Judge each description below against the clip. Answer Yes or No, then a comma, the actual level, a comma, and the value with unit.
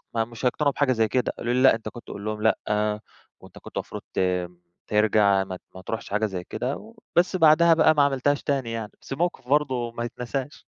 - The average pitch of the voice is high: No, low, 120 Hz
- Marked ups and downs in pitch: No, average, 4.8 semitones